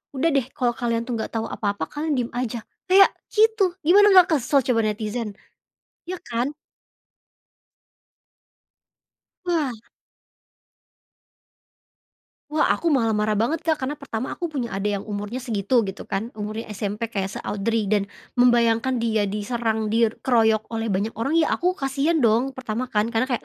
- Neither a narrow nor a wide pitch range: Yes, average, 4.1 semitones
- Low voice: No, high, 235 Hz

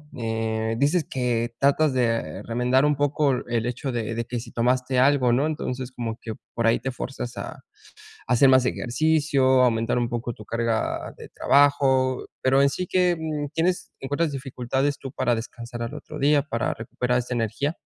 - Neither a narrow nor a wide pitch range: Yes, average, 3.2 semitones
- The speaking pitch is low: Yes, low, 125 Hz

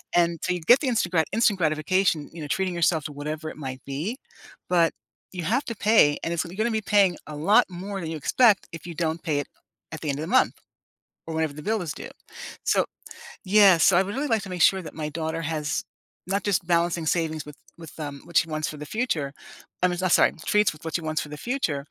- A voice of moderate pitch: Yes, medium, 170 Hz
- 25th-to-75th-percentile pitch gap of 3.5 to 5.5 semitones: Yes, average, 3.9 semitones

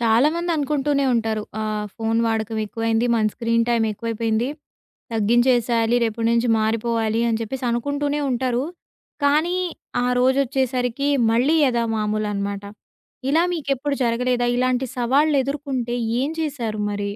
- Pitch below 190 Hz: No, high, 240 Hz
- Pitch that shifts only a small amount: No, average, 3.3 semitones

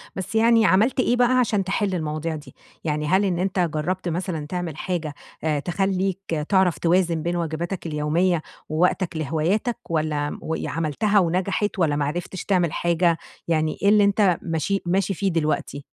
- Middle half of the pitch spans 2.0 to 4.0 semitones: Yes, average, 3.6 semitones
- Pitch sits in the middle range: Yes, medium, 175 Hz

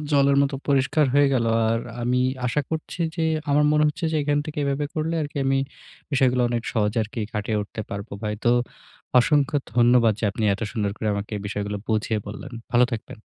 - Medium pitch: No, low, 125 Hz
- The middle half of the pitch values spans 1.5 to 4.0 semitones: No, average, 4.7 semitones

